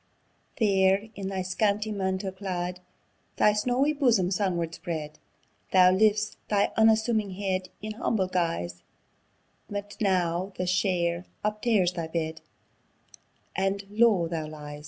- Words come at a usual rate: No, slow, 125 wpm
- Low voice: No, high, 190 Hz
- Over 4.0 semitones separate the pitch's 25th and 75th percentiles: No, average, 3.1 semitones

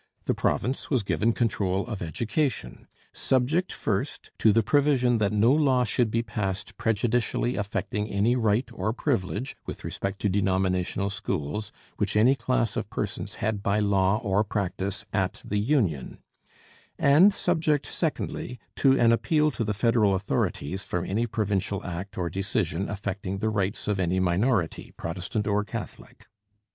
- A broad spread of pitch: No, average, 3.6 semitones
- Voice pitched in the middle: No, low, 105 Hz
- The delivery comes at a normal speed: Yes, average, 150 wpm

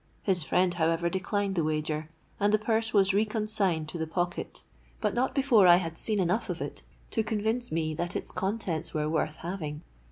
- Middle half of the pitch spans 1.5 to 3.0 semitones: No, average, 4.7 semitones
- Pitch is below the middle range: No, medium, 185 Hz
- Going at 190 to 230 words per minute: Yes, average, 195 wpm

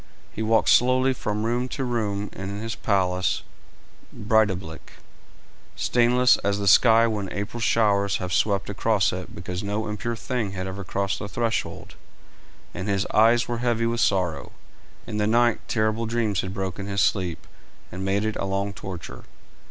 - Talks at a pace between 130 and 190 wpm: Yes, average, 160 wpm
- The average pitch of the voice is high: No, low, 105 Hz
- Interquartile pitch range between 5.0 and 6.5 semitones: No, average, 2.9 semitones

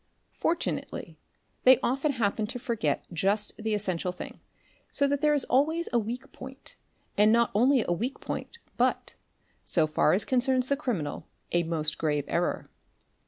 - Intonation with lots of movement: Yes, wide, 6.8 semitones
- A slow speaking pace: No, average, 165 wpm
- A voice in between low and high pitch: No, high, 230 Hz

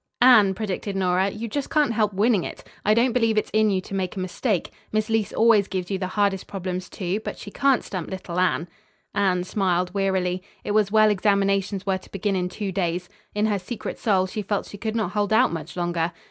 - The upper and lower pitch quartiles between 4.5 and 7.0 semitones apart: No, average, 2.7 semitones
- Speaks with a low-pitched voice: No, high, 195 Hz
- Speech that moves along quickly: Yes, fast, 220 wpm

